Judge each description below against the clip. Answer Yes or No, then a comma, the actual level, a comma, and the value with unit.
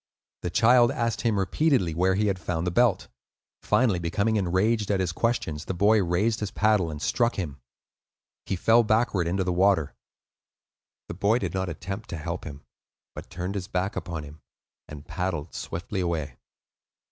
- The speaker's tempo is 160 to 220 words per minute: Yes, average, 170 wpm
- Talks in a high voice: No, very low, 95 Hz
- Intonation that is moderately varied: Yes, average, 4.1 semitones